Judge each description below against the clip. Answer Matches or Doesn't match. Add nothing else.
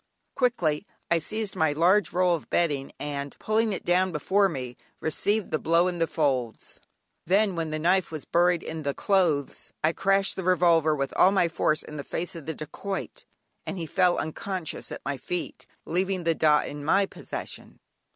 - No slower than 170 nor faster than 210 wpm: Matches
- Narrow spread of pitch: Doesn't match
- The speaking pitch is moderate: Matches